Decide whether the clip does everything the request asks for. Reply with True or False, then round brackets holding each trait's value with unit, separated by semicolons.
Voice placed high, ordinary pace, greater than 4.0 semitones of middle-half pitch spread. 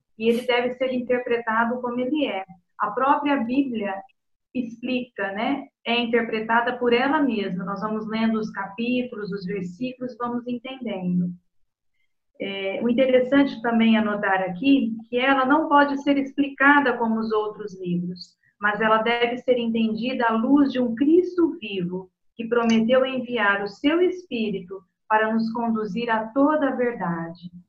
False (235 Hz; 145 wpm; 3.7 semitones)